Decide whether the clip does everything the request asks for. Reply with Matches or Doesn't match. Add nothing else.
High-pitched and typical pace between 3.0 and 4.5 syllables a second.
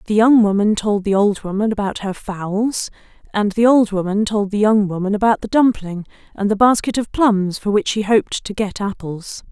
Doesn't match